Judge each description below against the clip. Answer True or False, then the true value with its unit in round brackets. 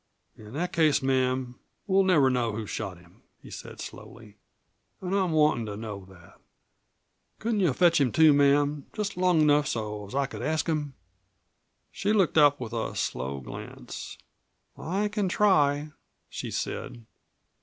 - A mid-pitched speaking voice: True (145 Hz)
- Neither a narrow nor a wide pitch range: False (6.9 semitones)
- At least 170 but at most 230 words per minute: False (155 wpm)